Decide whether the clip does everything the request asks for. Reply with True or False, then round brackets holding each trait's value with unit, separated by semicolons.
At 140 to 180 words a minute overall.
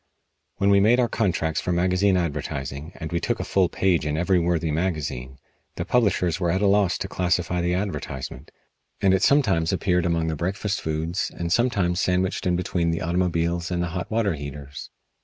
False (190 wpm)